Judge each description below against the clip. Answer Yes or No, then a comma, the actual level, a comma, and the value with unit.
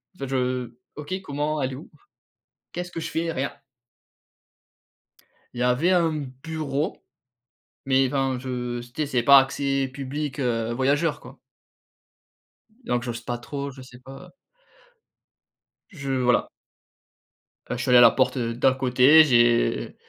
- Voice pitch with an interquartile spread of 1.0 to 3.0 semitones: Yes, narrow, 2.6 semitones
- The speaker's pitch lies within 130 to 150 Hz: Yes, low, 135 Hz